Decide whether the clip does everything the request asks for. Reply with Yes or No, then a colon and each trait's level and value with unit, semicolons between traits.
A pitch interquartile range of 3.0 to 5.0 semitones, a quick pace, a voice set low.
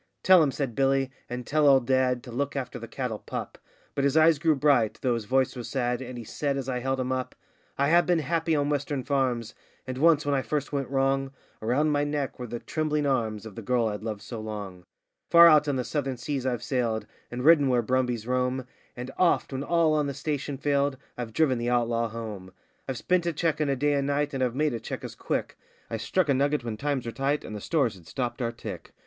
Yes: average, 3.3 semitones; fast, 240 wpm; low, 130 Hz